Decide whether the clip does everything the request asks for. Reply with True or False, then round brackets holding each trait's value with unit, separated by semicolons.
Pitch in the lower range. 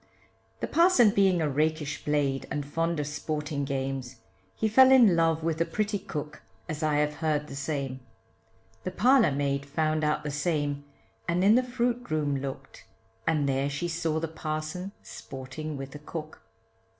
False (155 Hz)